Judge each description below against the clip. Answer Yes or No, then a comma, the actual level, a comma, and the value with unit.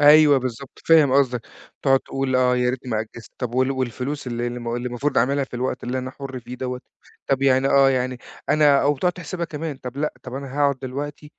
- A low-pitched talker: Yes, low, 130 Hz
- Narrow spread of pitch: Yes, narrow, 2.1 semitones